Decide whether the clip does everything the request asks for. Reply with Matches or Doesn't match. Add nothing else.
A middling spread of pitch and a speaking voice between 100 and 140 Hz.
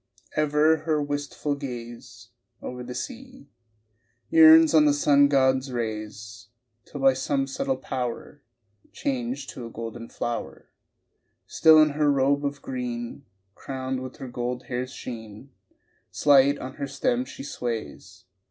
Matches